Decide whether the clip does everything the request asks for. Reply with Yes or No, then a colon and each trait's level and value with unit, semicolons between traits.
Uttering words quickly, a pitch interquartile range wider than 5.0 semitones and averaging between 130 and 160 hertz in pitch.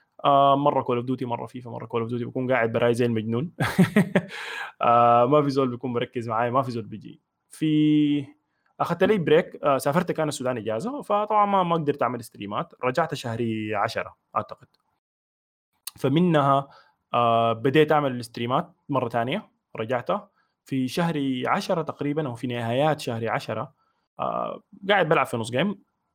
Yes: fast, 150 wpm; wide, 5.4 semitones; low, 135 Hz